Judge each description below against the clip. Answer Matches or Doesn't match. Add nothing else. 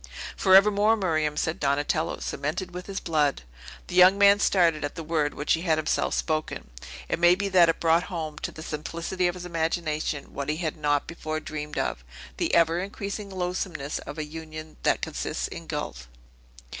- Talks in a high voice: Doesn't match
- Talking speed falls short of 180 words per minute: Doesn't match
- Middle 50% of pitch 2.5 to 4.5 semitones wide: Matches